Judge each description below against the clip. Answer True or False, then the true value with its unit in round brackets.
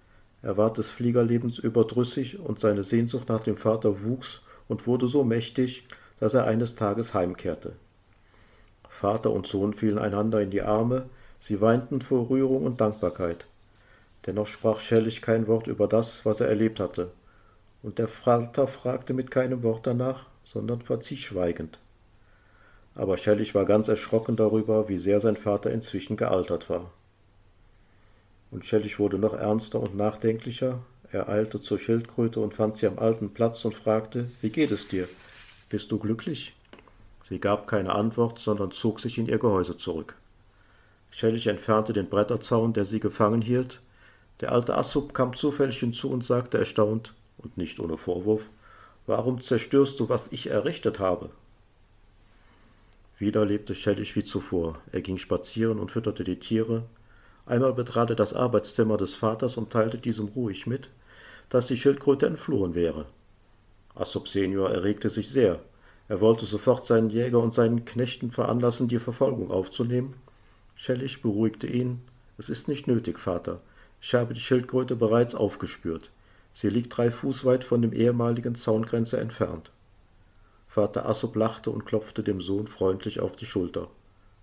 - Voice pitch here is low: True (110 Hz)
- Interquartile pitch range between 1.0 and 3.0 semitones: True (2.7 semitones)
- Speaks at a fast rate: False (155 wpm)